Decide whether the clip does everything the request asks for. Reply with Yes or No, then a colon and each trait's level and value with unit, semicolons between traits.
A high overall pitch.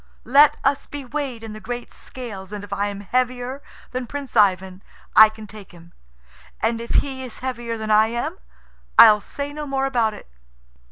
Yes: high, 235 Hz